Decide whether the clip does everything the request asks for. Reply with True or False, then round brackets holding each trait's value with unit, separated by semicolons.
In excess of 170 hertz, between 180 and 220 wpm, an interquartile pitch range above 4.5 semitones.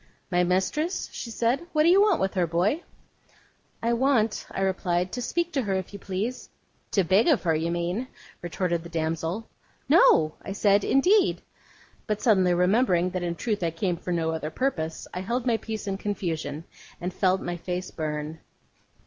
True (190 Hz; 185 wpm; 5.2 semitones)